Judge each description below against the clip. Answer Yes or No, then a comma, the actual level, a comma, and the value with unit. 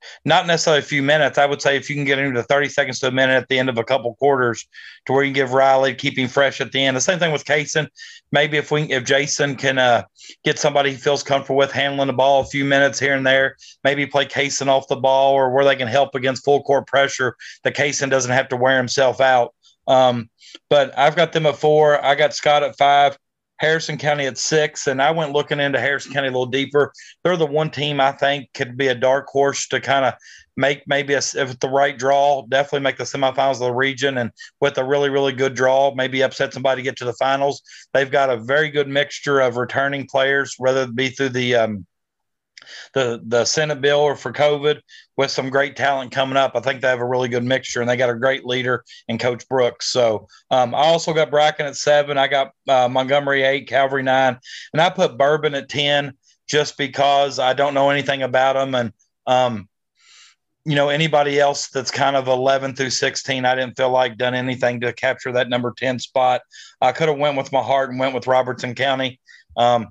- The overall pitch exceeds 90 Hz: Yes, low, 135 Hz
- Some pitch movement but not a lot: No, narrow, 1.6 semitones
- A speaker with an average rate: No, fast, 230 wpm